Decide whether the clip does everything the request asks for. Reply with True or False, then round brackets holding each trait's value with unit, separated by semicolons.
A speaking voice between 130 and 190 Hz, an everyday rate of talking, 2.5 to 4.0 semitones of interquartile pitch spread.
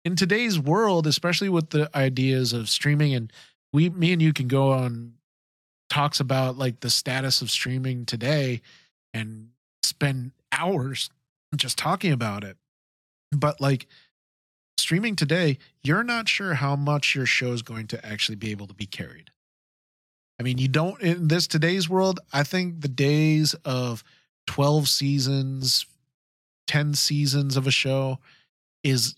True (140 Hz; 150 wpm; 3.6 semitones)